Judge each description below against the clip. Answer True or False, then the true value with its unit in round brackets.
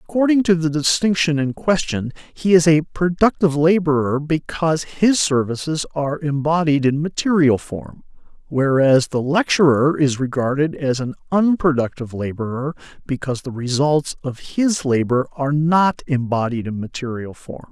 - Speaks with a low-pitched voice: False (145 Hz)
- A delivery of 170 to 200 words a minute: False (135 wpm)